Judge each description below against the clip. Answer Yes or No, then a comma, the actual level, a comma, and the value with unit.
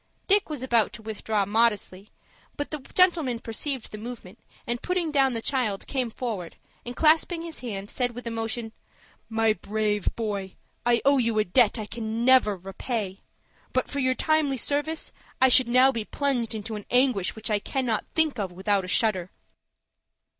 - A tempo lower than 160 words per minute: No, average, 175 wpm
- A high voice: Yes, high, 235 Hz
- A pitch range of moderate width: Yes, average, 3.9 semitones